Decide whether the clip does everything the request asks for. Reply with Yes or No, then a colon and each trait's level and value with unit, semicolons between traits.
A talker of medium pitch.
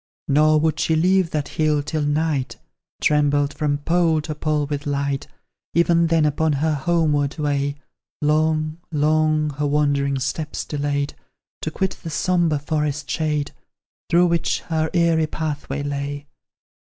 Yes: medium, 150 Hz